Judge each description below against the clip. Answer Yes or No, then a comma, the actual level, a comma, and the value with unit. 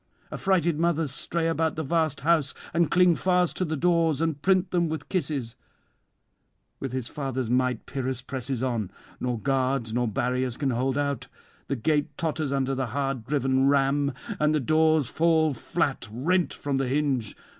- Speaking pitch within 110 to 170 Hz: Yes, medium, 140 Hz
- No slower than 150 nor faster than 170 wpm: Yes, average, 165 wpm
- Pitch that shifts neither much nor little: Yes, average, 3.7 semitones